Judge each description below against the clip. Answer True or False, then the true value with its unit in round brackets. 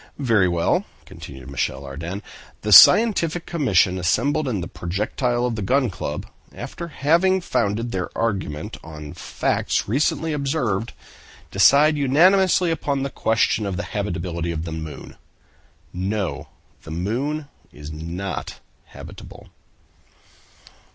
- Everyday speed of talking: False (115 wpm)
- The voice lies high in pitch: False (105 Hz)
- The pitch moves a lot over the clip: True (8.5 semitones)